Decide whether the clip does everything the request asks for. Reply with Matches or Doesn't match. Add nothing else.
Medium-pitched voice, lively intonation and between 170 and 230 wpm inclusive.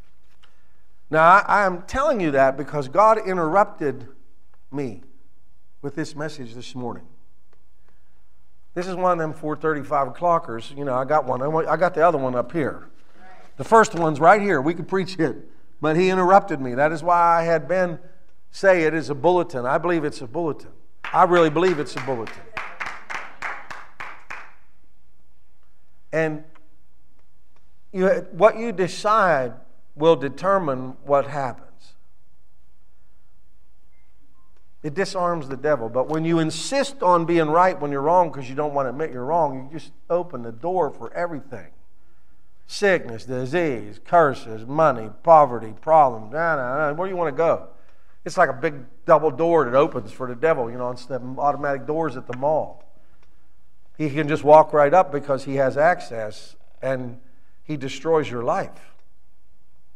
Doesn't match